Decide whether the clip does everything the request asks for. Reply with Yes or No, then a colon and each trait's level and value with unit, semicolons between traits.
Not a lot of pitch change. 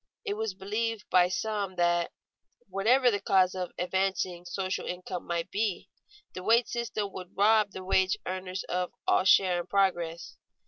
Yes: narrow, 2.3 semitones